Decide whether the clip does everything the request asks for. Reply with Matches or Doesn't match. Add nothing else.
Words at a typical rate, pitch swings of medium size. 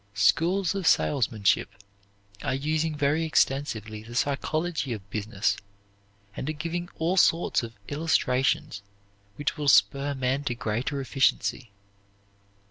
Doesn't match